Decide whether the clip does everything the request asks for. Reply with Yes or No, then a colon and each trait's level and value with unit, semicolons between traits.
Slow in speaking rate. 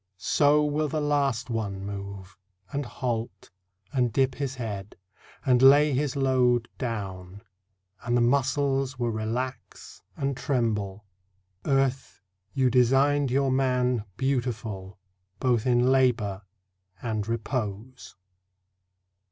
Yes: slow, 110 wpm